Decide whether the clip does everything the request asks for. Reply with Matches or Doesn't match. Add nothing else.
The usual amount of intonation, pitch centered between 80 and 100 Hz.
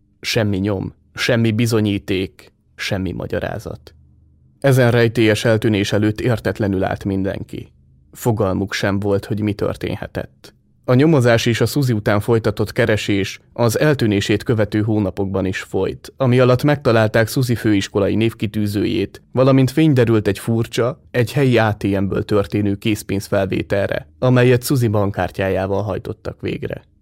Doesn't match